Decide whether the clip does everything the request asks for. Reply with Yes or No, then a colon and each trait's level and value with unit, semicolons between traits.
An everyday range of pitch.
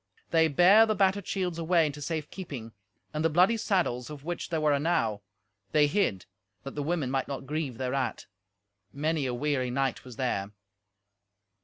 Yes: average, 4.6 semitones